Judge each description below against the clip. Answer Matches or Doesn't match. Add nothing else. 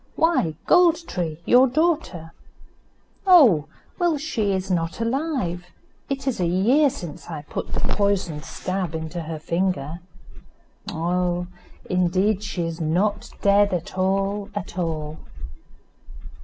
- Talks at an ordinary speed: Doesn't match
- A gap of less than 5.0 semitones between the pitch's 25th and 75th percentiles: Doesn't match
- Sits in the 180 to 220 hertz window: Matches